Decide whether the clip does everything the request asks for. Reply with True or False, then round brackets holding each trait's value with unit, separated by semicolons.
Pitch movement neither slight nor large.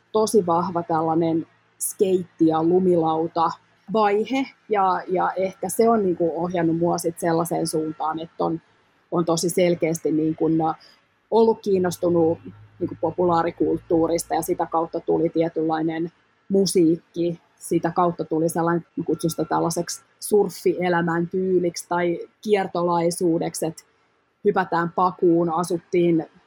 False (1.8 semitones)